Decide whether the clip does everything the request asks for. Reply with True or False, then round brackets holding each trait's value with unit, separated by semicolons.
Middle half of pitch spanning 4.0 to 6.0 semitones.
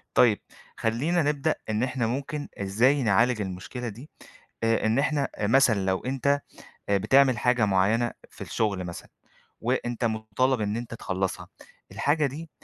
True (4.5 semitones)